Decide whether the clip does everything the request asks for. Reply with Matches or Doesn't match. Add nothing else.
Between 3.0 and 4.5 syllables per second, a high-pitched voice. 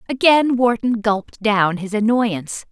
Matches